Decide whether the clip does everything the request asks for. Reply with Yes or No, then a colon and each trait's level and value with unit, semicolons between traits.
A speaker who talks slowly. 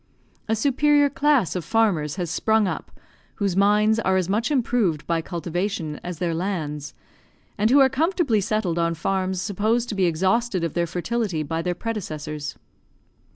No: average, 160 wpm